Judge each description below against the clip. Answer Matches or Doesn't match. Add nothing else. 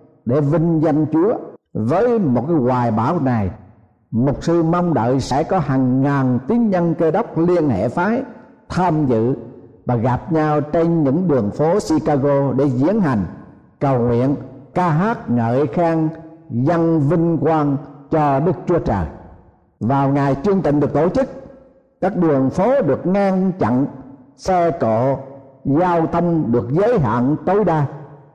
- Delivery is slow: Matches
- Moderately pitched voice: Matches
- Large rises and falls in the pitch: Doesn't match